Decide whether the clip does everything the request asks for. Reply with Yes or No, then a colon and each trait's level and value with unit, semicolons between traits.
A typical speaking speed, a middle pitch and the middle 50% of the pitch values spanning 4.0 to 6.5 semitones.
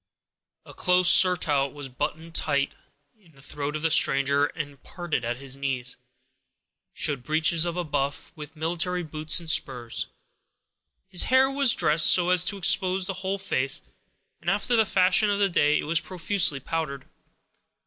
Yes: average, 160 wpm; medium, 160 Hz; average, 4.4 semitones